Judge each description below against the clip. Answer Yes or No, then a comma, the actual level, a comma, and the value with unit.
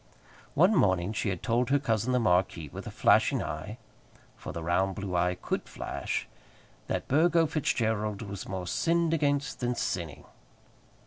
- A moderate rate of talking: Yes, average, 155 wpm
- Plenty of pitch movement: Yes, wide, 7.3 semitones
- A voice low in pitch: Yes, low, 110 Hz